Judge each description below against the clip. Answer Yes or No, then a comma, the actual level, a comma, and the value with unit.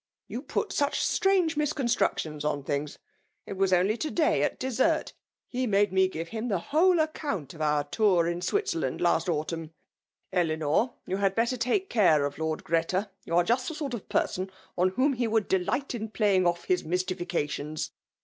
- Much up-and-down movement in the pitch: Yes, wide, 7.2 semitones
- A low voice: No, high, 190 Hz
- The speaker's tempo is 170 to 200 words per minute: Yes, average, 185 wpm